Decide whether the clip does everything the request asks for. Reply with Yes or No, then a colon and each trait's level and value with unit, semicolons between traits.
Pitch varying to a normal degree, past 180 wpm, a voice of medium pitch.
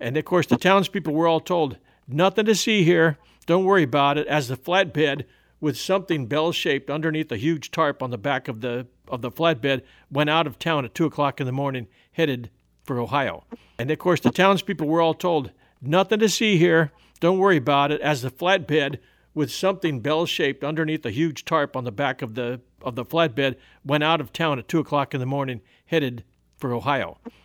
Yes: average, 3.8 semitones; fast, 205 wpm; medium, 150 Hz